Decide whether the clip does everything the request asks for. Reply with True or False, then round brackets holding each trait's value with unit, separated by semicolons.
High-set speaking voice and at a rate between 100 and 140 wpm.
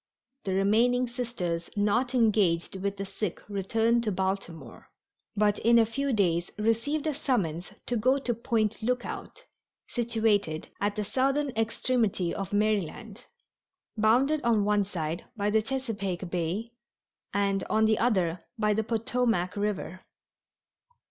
True (215 Hz; 135 wpm)